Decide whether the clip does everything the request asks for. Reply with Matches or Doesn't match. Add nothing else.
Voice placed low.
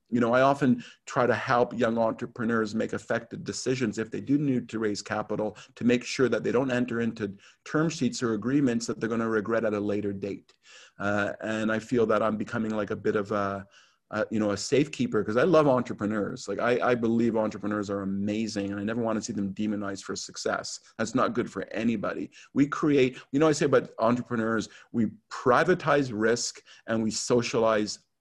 Matches